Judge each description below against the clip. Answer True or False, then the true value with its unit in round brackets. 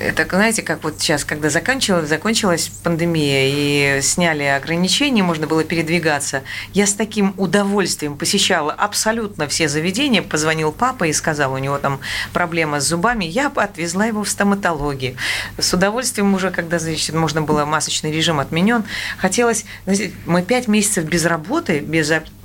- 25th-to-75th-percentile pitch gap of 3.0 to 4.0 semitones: False (4.4 semitones)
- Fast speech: False (145 wpm)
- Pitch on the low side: False (170 Hz)